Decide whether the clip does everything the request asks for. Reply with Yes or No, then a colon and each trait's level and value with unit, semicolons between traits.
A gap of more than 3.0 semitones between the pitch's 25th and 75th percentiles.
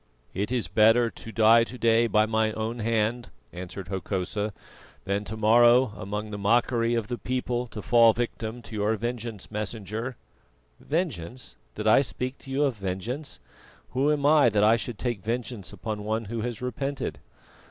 No: narrow, 2.4 semitones